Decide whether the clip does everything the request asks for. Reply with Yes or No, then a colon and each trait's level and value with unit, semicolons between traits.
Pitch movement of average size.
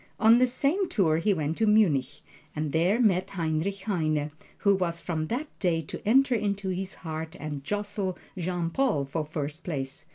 Yes: average, 4.8 semitones